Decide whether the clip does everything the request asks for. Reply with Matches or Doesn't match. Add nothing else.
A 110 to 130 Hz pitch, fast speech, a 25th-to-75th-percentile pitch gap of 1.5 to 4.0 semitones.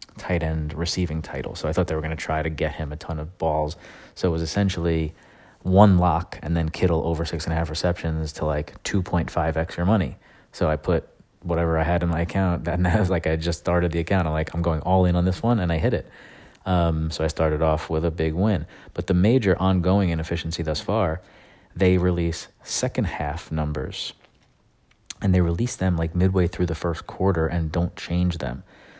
Doesn't match